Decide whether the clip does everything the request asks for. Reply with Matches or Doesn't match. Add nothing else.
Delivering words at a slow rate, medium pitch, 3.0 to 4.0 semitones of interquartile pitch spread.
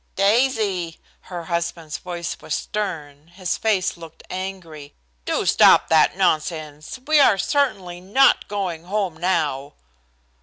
Matches